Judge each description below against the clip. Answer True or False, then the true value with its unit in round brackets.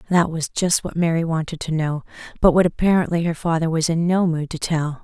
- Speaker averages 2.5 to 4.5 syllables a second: False (5.6 syllables/s)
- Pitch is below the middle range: False (165 Hz)